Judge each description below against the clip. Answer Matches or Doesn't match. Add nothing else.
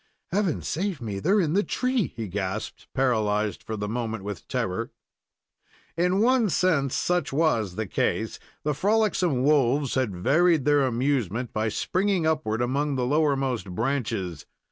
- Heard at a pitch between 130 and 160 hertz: Matches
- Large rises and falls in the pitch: Matches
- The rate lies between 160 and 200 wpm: Doesn't match